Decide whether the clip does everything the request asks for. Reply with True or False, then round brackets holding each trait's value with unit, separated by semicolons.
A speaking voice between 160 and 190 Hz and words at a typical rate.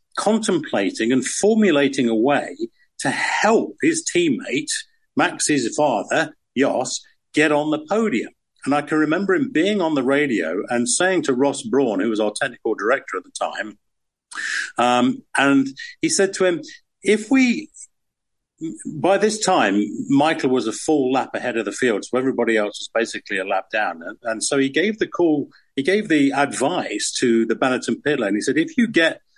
True (185 Hz; 180 wpm)